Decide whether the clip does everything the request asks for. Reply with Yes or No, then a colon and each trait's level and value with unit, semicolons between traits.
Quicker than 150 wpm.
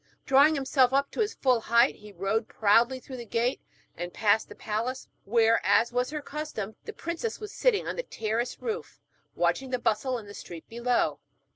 Yes: average, 190 wpm